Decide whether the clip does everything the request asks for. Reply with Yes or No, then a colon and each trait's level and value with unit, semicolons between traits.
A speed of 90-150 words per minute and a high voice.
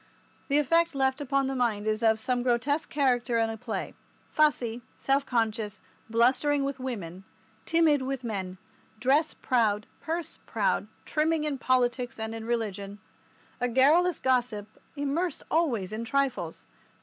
Yes: average, 140 wpm; very high, 255 Hz